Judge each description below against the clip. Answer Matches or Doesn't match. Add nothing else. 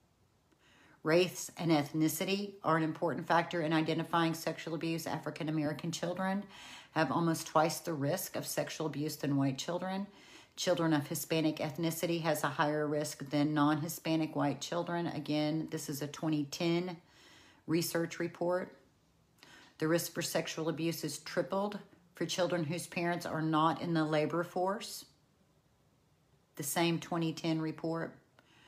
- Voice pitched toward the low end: Doesn't match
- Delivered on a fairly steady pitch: Matches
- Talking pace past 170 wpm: Doesn't match